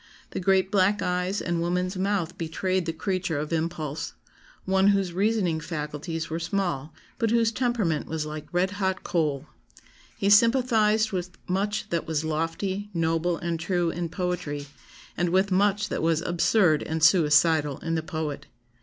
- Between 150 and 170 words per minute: Yes, average, 155 wpm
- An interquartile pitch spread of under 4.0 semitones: Yes, average, 3.3 semitones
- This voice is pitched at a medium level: Yes, medium, 175 Hz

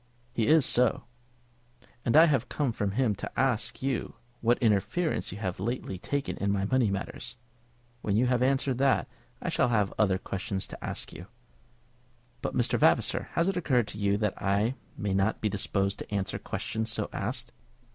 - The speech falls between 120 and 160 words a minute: No, average, 180 wpm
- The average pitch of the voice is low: Yes, low, 110 Hz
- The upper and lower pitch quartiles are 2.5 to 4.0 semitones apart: No, average, 4.4 semitones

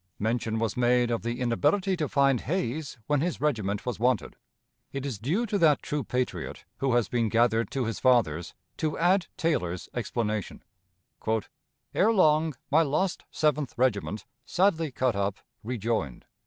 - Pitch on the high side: No, low, 125 Hz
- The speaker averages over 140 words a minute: Yes, average, 155 wpm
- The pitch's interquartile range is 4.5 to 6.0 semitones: Yes, average, 5.1 semitones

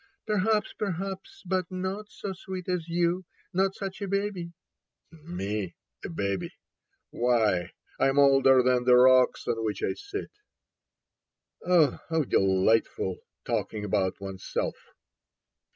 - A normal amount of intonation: No, wide, 9.0 semitones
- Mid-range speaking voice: Yes, medium, 160 Hz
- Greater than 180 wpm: No, slow, 135 wpm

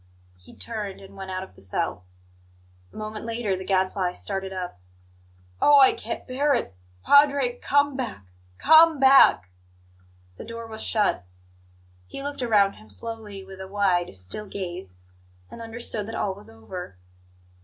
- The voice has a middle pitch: No, high, 205 Hz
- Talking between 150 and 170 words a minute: Yes, average, 155 wpm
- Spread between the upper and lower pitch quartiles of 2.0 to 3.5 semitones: No, average, 4.3 semitones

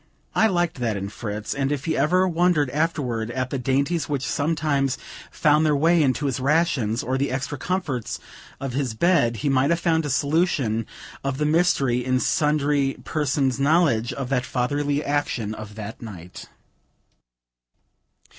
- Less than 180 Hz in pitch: Yes, medium, 140 Hz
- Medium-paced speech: Yes, average, 160 wpm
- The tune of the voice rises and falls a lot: No, average, 3.7 semitones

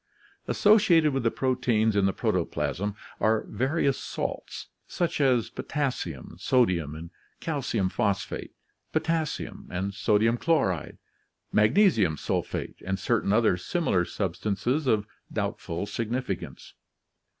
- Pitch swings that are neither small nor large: No, wide, 5.9 semitones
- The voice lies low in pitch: Yes, low, 110 Hz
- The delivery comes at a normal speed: No, slow, 105 wpm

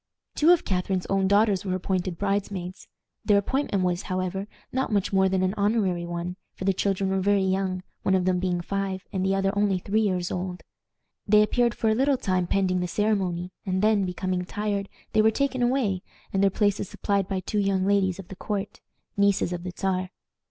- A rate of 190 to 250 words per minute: Yes, average, 200 wpm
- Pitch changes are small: Yes, narrow, 1.8 semitones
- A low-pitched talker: No, high, 195 Hz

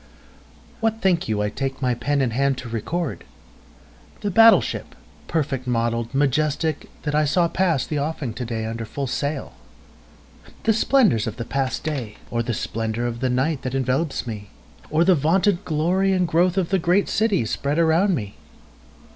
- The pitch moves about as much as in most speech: No, wide, 6.3 semitones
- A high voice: No, medium, 140 Hz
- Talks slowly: No, average, 165 wpm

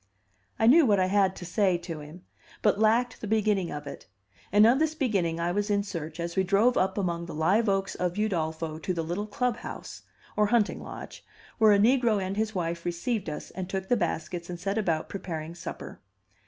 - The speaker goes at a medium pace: No, fast, 210 wpm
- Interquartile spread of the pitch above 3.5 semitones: Yes, average, 3.9 semitones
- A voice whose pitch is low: No, high, 190 Hz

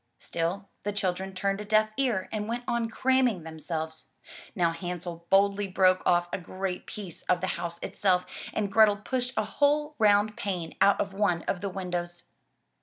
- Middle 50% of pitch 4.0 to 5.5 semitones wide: No, average, 3.1 semitones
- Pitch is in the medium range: No, high, 195 Hz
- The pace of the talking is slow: No, average, 180 wpm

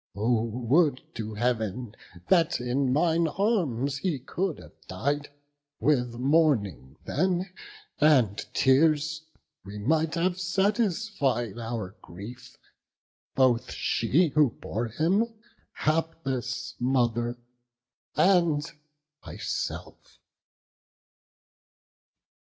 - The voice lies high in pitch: No, low, 135 Hz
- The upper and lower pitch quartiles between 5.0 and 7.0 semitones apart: Yes, wide, 5.4 semitones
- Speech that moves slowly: Yes, slow, 85 wpm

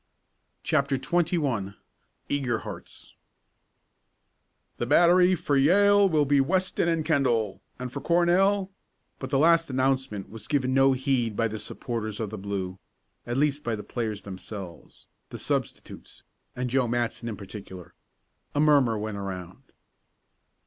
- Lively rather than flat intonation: Yes, wide, 5.9 semitones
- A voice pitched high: No, low, 130 Hz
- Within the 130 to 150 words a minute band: Yes, average, 140 wpm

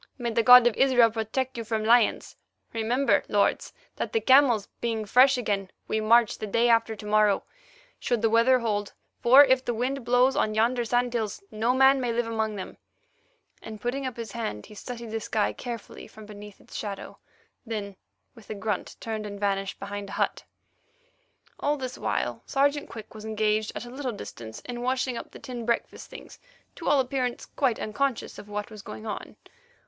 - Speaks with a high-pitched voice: Yes, high, 230 Hz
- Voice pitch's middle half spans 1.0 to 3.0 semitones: Yes, average, 2.7 semitones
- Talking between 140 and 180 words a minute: No, average, 190 wpm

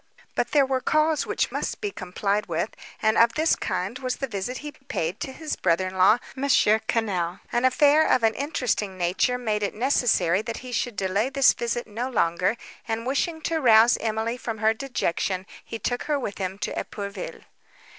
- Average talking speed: Yes, average, 190 wpm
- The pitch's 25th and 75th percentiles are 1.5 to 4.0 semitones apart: No, average, 4.7 semitones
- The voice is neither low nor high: No, high, 225 Hz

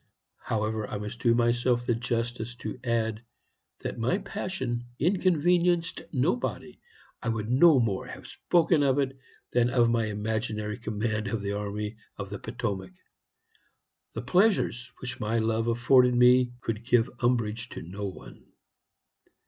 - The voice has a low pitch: Yes, low, 120 Hz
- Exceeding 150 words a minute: No, average, 140 wpm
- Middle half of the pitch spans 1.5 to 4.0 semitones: Yes, average, 2.8 semitones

